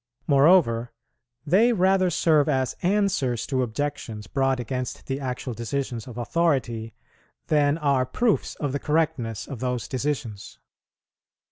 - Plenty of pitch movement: No, average, 4.3 semitones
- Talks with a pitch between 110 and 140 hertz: Yes, low, 135 Hz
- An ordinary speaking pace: No, slow, 125 wpm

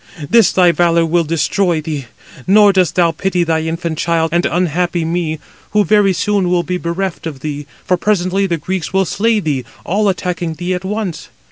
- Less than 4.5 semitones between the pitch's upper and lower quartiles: Yes, average, 2.7 semitones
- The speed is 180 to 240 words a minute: Yes, average, 190 wpm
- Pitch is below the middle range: No, medium, 175 Hz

